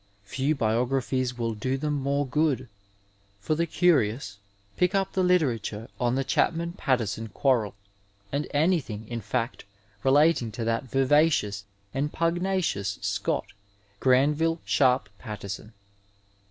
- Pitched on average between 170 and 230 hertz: No, low, 130 Hz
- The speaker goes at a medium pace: No, slow, 120 wpm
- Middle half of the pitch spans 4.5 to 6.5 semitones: Yes, average, 5.2 semitones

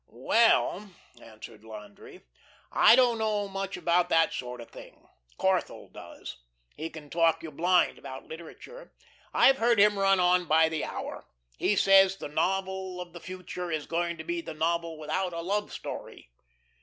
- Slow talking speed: No, average, 165 wpm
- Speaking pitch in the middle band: Yes, medium, 180 Hz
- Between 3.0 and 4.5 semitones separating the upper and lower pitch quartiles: Yes, average, 3.4 semitones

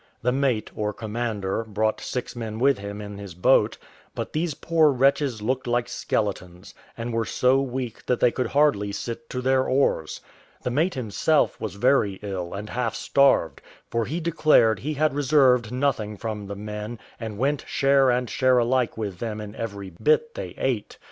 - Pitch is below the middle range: Yes, low, 120 Hz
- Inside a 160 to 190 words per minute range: Yes, average, 180 wpm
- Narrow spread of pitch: No, average, 4.3 semitones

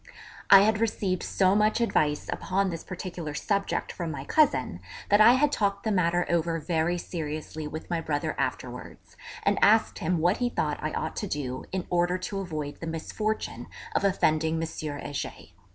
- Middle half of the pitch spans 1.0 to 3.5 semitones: No, average, 4.1 semitones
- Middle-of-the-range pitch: Yes, medium, 175 Hz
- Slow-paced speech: No, average, 175 wpm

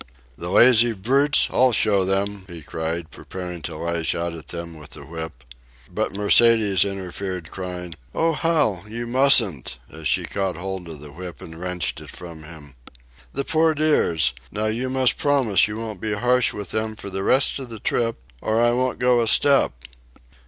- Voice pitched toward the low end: Yes, low, 100 Hz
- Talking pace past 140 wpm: Yes, average, 180 wpm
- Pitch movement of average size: No, wide, 5.8 semitones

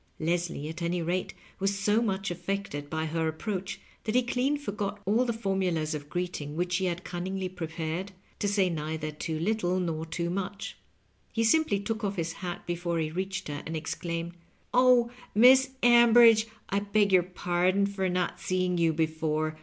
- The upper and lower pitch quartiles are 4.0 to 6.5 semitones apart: No, average, 3.6 semitones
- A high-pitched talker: No, medium, 180 Hz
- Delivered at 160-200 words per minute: Yes, average, 170 wpm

